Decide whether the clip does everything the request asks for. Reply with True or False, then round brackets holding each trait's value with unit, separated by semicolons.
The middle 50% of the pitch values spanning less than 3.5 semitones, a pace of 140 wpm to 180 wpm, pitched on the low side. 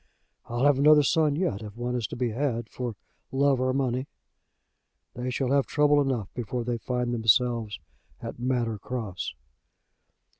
True (2.6 semitones; 155 wpm; 125 Hz)